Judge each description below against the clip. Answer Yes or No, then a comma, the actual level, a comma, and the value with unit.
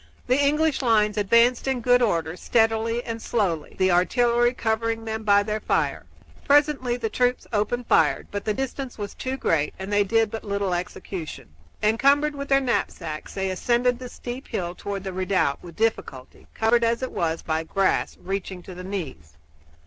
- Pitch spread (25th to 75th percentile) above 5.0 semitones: No, average, 4.6 semitones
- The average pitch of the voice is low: No, high, 220 Hz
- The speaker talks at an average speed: Yes, average, 175 wpm